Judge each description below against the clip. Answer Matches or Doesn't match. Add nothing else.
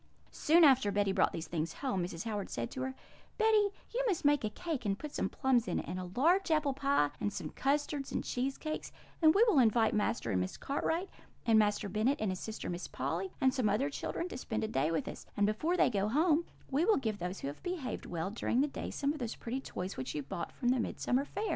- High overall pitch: Matches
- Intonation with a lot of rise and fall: Matches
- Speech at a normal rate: Doesn't match